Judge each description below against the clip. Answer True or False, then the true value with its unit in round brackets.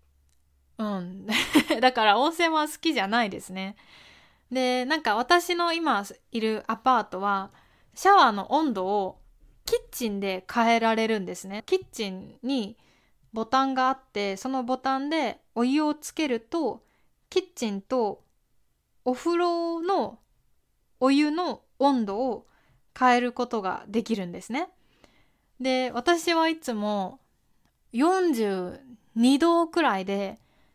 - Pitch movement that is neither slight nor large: False (6.4 semitones)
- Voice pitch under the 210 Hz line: False (250 Hz)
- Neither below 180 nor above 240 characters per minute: True (230 characters per minute)